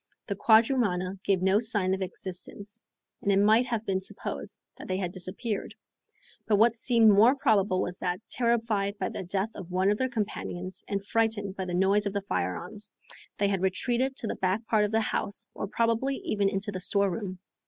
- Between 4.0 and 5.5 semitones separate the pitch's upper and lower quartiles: No, average, 2.9 semitones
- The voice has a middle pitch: No, high, 200 Hz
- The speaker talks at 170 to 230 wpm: Yes, average, 195 wpm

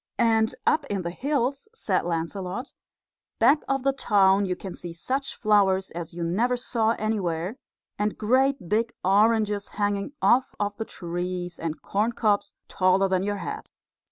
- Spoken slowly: No, average, 155 wpm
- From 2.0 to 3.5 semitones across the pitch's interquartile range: No, average, 4.2 semitones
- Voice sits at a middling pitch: No, high, 205 Hz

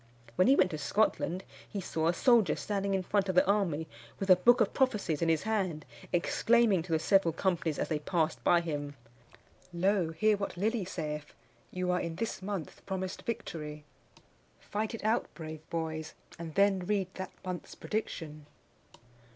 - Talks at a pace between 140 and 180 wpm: Yes, average, 175 wpm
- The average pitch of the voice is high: No, medium, 180 Hz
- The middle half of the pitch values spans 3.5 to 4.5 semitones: Yes, average, 4.0 semitones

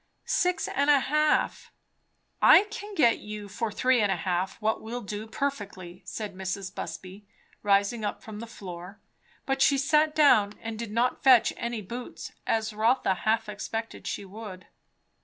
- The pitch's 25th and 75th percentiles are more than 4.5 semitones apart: No, average, 4.0 semitones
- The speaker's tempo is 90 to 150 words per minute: No, average, 160 wpm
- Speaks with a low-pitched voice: No, high, 220 Hz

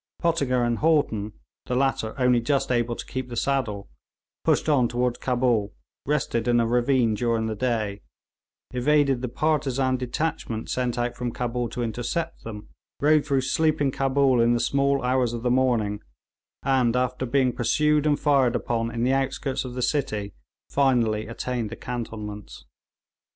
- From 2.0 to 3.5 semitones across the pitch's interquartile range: Yes, narrow, 2.6 semitones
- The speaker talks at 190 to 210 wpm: No, average, 160 wpm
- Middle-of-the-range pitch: No, low, 125 Hz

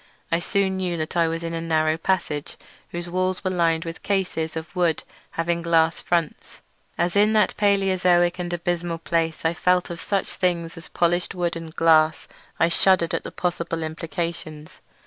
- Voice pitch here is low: No, medium, 170 Hz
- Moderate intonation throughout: No, narrow, 1.6 semitones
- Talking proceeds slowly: No, average, 175 wpm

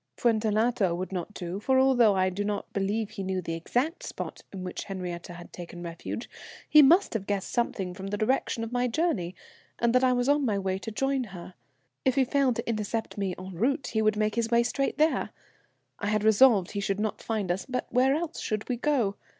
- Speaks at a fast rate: Yes, fast, 220 wpm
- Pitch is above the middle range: Yes, high, 215 Hz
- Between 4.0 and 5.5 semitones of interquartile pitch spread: Yes, average, 4.6 semitones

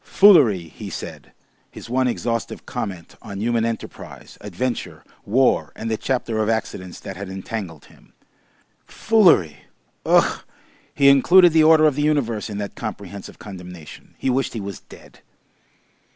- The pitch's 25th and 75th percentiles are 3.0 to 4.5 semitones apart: No, wide, 5.4 semitones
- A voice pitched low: Yes, low, 110 Hz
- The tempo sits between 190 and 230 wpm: No, average, 145 wpm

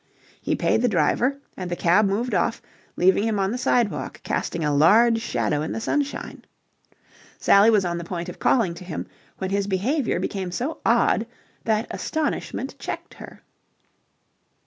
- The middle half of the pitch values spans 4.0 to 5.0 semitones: Yes, average, 4.7 semitones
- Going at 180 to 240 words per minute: No, average, 165 wpm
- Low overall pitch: No, high, 200 Hz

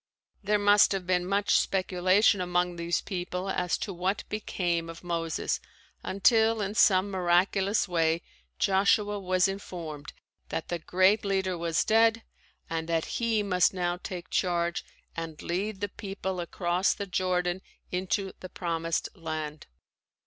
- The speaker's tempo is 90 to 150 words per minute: Yes, average, 140 wpm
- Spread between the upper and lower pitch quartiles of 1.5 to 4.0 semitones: Yes, narrow, 2.4 semitones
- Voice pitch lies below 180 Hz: No, medium, 185 Hz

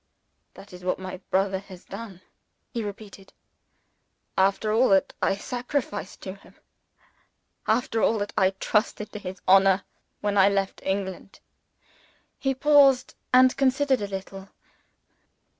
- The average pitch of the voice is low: No, high, 200 Hz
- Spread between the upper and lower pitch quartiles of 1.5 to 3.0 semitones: No, average, 3.4 semitones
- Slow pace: Yes, slow, 130 wpm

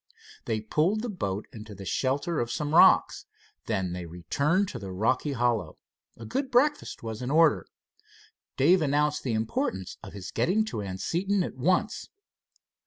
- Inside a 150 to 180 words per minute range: Yes, average, 160 wpm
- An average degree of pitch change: No, wide, 8.6 semitones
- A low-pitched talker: Yes, low, 130 Hz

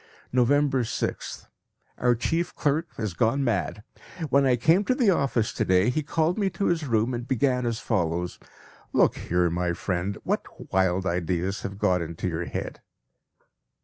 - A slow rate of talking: No, average, 165 wpm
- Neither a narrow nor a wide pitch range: No, wide, 7.4 semitones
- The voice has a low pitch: Yes, low, 115 Hz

